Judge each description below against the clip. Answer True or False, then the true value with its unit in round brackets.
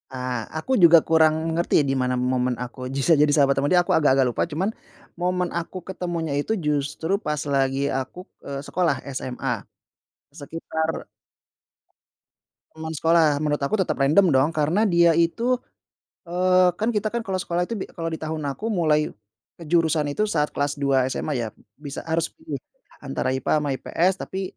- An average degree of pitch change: True (3.9 semitones)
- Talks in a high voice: False (160 Hz)